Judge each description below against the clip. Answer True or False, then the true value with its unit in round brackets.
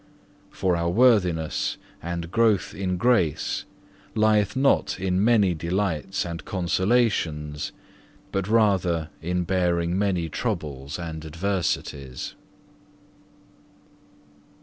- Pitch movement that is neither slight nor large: True (3.6 semitones)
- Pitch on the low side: True (90 Hz)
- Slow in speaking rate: True (90 wpm)